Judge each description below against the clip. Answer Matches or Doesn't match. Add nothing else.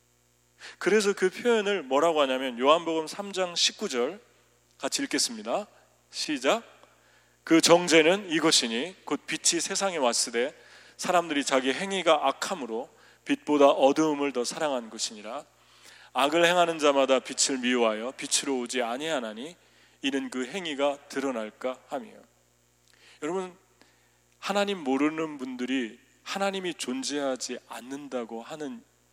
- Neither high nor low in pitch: Matches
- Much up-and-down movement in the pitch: Matches